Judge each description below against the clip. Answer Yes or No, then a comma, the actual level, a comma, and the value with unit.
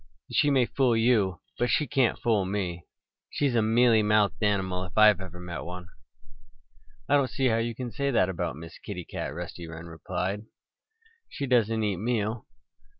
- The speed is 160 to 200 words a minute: Yes, average, 170 wpm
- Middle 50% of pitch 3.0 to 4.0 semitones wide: No, average, 4.8 semitones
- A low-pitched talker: Yes, low, 105 Hz